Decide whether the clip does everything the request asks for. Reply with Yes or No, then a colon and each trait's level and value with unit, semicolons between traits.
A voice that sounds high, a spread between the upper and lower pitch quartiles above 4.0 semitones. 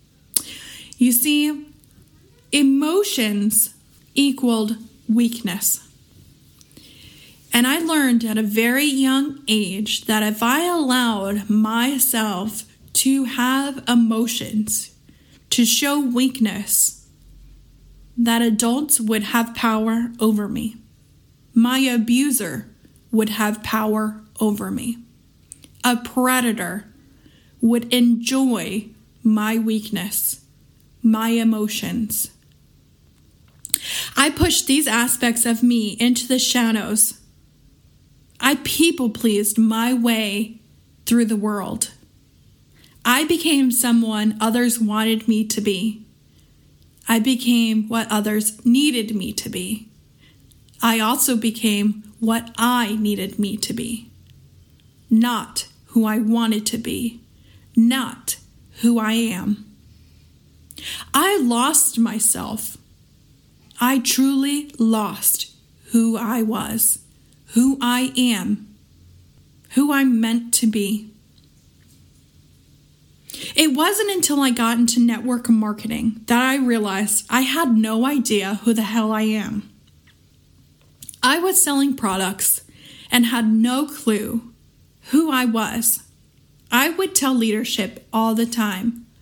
No: high, 230 Hz; narrow, 2.4 semitones